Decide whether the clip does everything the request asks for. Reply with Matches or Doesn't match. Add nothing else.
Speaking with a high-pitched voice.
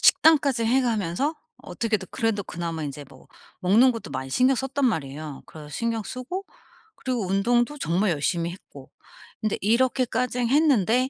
Matches